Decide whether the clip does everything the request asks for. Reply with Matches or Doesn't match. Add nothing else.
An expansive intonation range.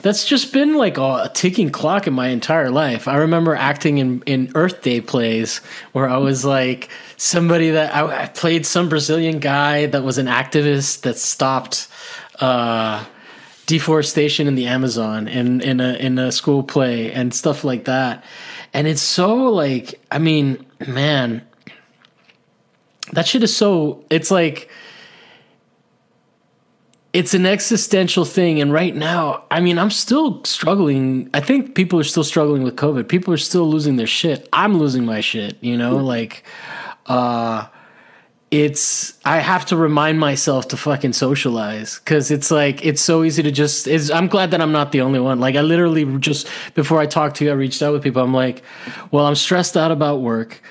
Doesn't match